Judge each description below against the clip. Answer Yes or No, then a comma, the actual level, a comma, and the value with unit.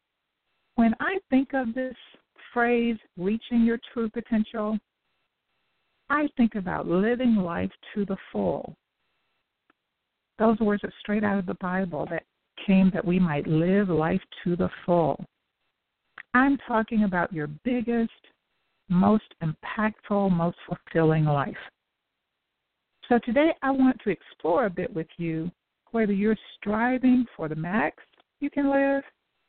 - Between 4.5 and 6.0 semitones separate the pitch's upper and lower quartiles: Yes, average, 5.1 semitones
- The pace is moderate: No, slow, 130 wpm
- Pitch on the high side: Yes, high, 215 Hz